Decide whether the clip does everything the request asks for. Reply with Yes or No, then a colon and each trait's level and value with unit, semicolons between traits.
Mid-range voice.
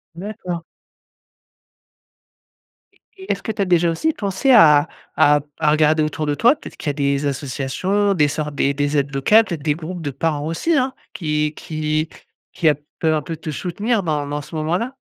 Yes: medium, 155 Hz